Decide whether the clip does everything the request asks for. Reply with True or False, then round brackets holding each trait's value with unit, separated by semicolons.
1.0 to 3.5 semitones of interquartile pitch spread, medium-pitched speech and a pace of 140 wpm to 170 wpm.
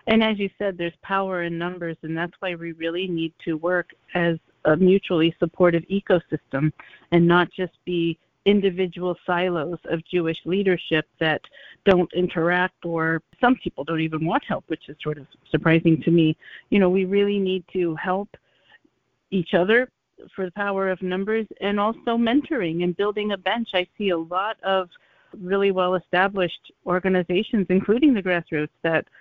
True (2.6 semitones; 180 Hz; 165 wpm)